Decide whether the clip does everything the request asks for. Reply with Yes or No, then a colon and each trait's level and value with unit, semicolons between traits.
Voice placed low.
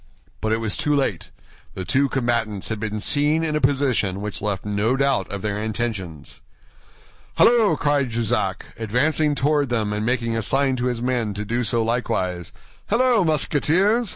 Yes: low, 120 Hz